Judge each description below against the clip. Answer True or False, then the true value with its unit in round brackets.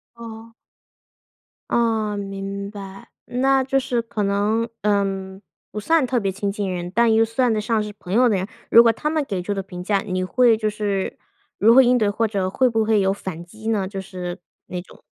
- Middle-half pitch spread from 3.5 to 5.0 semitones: False (2.8 semitones)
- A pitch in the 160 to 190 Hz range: False (210 Hz)